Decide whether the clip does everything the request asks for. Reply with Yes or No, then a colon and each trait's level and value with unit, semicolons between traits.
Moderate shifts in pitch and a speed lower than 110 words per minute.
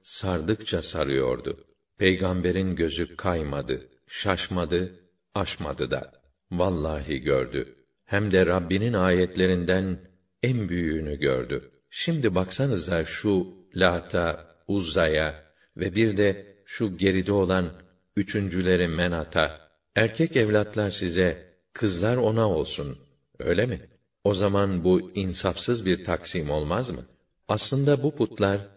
No: narrow, 2.3 semitones; average, 100 wpm